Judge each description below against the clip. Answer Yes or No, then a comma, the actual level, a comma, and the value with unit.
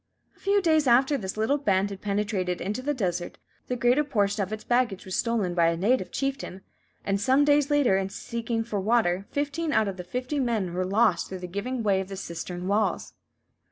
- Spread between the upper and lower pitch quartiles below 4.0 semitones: No, average, 5.2 semitones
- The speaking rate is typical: No, fast, 210 wpm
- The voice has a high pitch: Yes, high, 210 Hz